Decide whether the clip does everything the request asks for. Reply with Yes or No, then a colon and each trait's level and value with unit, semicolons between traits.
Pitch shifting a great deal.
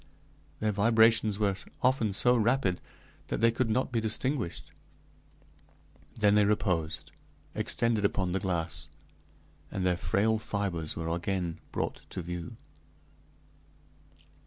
No: average, 4.1 semitones